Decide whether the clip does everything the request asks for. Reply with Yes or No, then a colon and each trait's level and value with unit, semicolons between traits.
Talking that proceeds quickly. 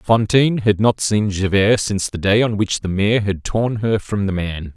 Yes: fast, 225 wpm